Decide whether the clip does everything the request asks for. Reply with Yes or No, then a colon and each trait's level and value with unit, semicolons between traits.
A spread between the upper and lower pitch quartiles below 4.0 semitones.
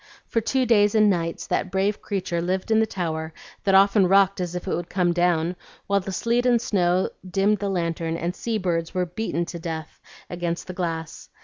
Yes: average, 3.0 semitones